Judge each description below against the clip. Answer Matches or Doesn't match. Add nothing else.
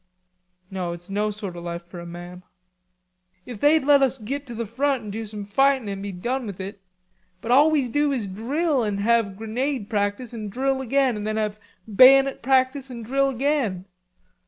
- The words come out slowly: Doesn't match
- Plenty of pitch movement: Doesn't match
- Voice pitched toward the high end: Matches